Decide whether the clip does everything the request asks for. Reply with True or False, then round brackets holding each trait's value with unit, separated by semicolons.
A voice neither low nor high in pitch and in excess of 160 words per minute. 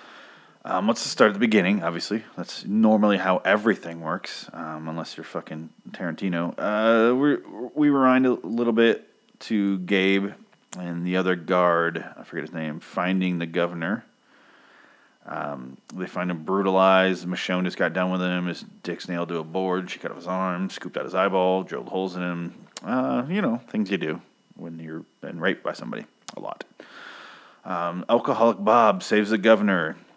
False (95 Hz; 175 wpm)